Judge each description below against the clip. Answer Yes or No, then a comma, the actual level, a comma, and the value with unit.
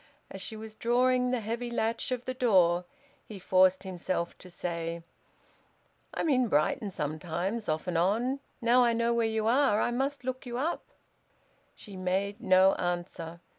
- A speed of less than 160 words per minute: No, average, 165 wpm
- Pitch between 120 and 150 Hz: No, high, 215 Hz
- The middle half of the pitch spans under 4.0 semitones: No, average, 5.1 semitones